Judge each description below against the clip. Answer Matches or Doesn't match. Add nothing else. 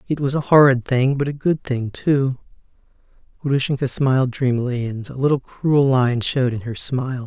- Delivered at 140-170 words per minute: Doesn't match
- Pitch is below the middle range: Matches